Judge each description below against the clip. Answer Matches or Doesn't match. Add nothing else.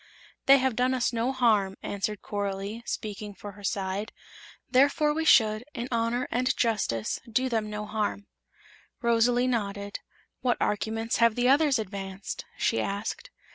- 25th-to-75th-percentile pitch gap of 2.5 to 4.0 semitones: Matches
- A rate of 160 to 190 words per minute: Doesn't match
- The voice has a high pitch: Matches